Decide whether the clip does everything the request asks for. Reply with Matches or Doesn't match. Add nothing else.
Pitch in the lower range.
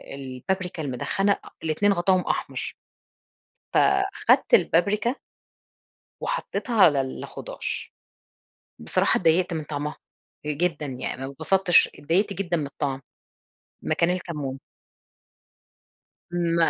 Doesn't match